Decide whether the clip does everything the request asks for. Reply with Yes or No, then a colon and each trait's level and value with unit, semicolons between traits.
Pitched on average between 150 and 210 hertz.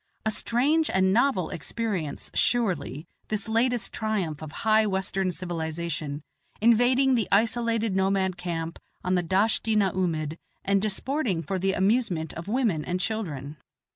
Yes: high, 190 Hz